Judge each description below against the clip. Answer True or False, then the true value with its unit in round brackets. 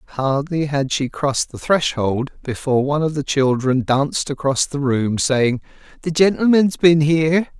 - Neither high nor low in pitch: True (145 Hz)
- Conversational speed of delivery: True (160 wpm)